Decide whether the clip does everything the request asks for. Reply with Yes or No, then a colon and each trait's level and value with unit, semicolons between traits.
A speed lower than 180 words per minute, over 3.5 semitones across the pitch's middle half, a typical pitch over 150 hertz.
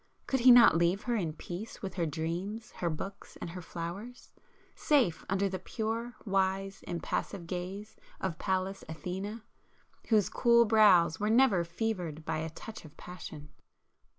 Yes: average, 150 wpm; average, 4.3 semitones; high, 190 Hz